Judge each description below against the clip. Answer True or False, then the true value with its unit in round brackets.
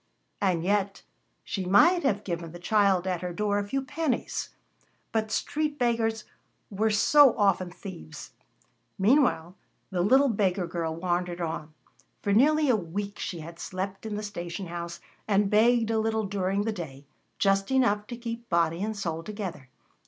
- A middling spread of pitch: True (4.1 semitones)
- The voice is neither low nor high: False (200 Hz)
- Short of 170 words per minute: True (160 wpm)